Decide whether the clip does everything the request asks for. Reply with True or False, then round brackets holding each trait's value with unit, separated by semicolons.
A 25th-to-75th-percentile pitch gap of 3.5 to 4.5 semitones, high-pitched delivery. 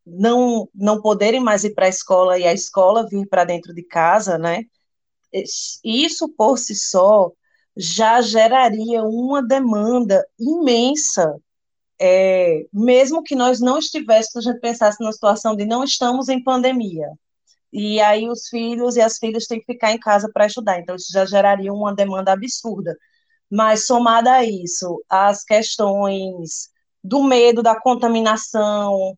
True (4.1 semitones; 220 Hz)